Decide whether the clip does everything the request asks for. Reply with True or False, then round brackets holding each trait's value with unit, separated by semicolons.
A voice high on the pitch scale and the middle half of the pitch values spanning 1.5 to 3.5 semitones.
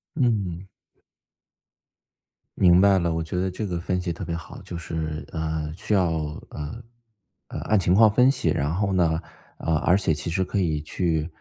False (90 Hz; 3.1 semitones)